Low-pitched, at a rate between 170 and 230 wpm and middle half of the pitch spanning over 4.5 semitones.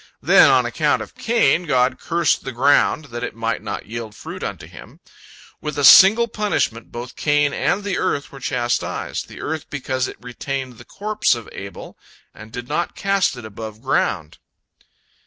Yes: low, 130 Hz; average, 175 wpm; wide, 5.4 semitones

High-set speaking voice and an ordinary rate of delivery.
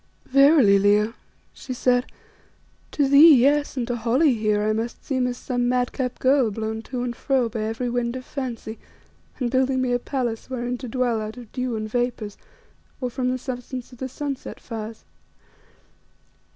Yes: high, 245 Hz; average, 175 wpm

